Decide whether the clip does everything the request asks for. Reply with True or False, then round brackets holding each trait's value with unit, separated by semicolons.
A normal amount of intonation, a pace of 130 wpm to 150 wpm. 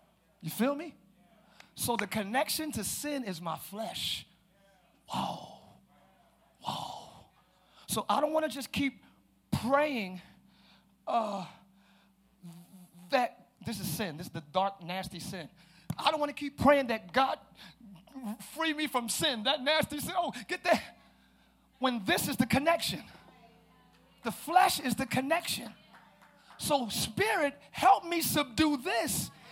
False (7.0 semitones; 135 wpm)